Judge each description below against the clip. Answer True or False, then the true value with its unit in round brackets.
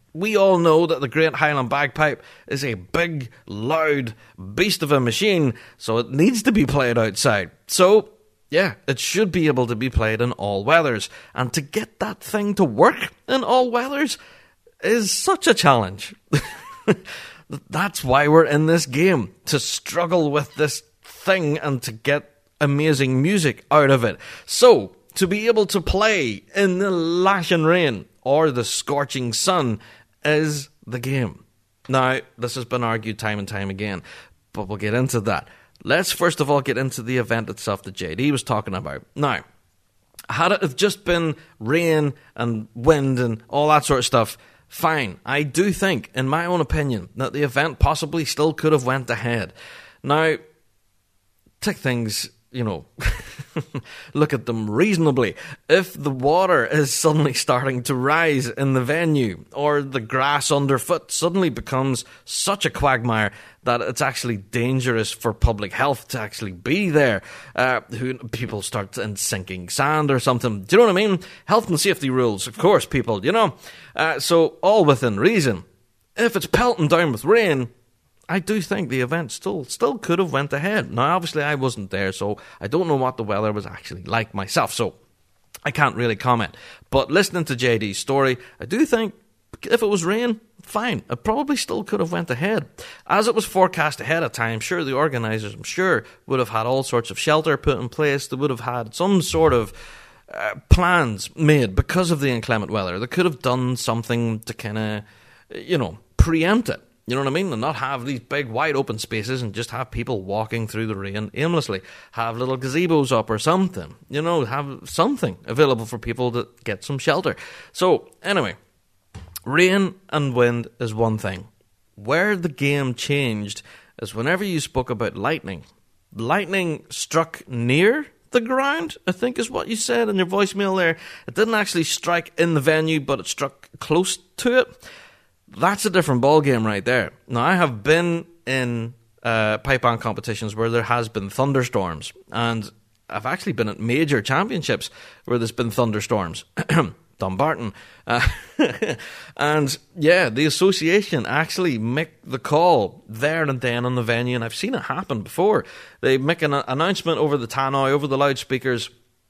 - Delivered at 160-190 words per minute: True (175 wpm)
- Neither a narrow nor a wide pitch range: False (5.9 semitones)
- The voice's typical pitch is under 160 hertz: True (135 Hz)